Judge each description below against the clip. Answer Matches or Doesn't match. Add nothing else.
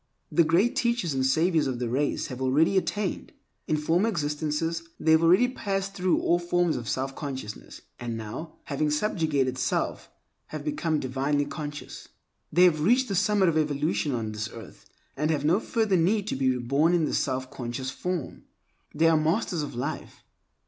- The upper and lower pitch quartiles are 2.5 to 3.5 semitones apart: Doesn't match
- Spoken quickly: Doesn't match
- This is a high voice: Doesn't match